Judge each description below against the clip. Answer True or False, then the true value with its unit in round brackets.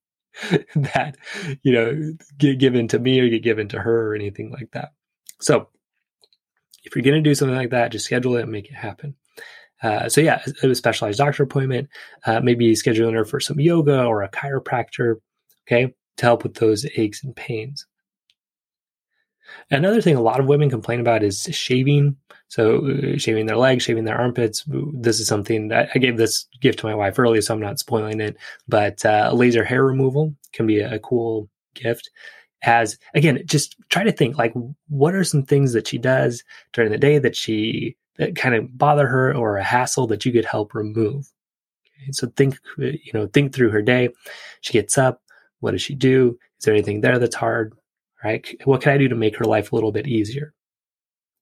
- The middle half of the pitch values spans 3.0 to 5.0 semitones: True (4.0 semitones)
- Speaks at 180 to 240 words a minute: True (195 wpm)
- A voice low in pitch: True (125 Hz)